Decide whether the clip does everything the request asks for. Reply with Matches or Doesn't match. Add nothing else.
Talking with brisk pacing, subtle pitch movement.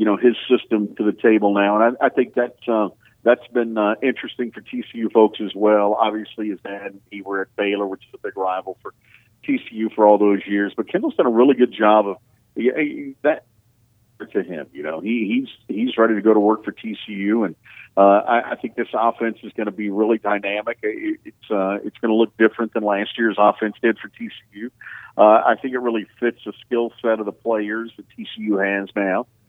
Matches